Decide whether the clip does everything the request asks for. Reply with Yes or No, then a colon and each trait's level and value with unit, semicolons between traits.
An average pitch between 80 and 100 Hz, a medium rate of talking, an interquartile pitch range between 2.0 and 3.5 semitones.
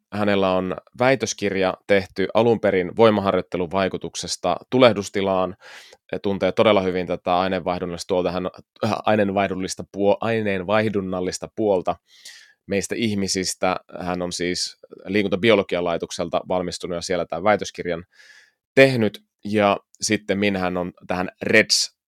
Yes: very low, 95 Hz; average, 105 wpm; narrow, 2.4 semitones